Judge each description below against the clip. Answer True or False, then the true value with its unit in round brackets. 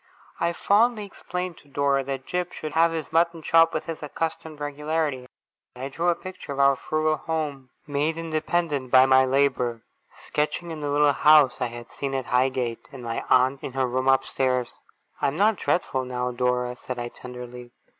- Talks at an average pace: True (185 wpm)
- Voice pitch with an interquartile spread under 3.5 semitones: False (3.9 semitones)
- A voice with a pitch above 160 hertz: False (140 Hz)